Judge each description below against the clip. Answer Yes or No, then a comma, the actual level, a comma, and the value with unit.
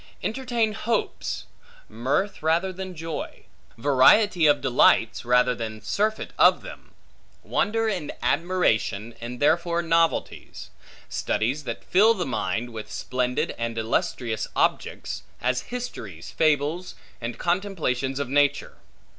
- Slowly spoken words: Yes, slow, 115 wpm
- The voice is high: No, medium, 145 Hz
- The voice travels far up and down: Yes, wide, 7.4 semitones